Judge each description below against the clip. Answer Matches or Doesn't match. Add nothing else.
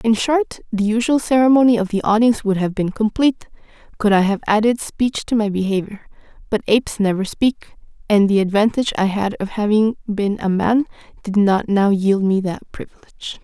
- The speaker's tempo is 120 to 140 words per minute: Doesn't match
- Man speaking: Doesn't match